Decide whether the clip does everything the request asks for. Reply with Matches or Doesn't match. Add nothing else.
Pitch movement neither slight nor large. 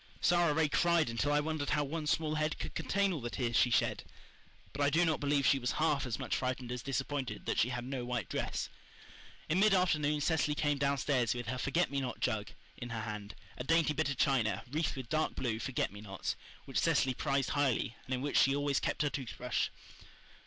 Matches